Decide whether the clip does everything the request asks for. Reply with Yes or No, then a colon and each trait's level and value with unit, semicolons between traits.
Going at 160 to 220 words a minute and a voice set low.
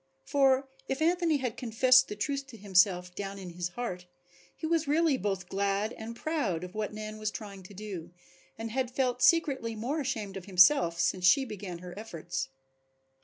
No: average, 180 wpm; high, 215 Hz